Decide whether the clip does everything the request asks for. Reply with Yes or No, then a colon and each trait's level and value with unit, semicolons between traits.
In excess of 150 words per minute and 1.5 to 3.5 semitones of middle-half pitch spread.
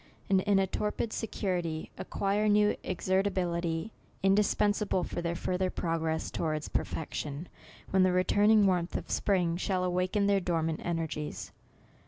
No: slow, 135 wpm; average, 3.0 semitones